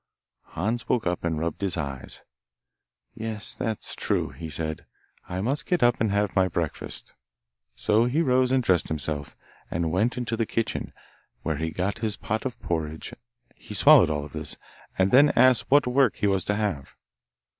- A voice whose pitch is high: No, low, 105 Hz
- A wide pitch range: Yes, wide, 6.6 semitones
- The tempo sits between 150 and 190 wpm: Yes, average, 175 wpm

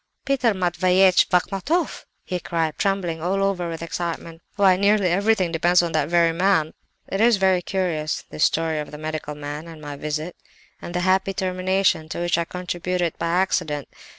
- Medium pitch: Yes, medium, 175 Hz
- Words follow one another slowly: No, average, 175 wpm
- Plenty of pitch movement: No, average, 2.8 semitones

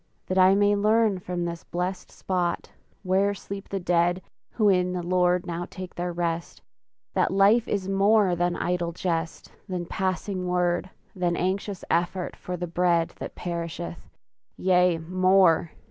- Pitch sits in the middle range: Yes, medium, 180 Hz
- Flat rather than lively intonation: Yes, narrow, 1.7 semitones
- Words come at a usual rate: Yes, average, 150 wpm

